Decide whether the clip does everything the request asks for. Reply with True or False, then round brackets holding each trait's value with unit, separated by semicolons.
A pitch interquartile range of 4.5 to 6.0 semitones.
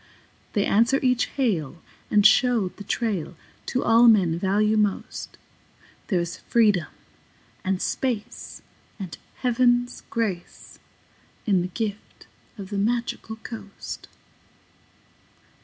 False (3.7 semitones)